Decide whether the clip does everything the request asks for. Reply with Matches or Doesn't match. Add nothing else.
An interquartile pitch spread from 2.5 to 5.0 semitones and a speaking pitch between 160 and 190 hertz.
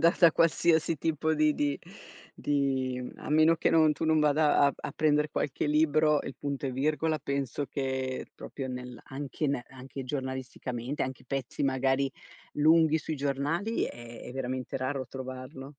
Doesn't match